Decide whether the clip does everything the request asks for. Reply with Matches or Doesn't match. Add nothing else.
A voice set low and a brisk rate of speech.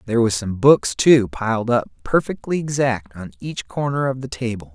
Doesn't match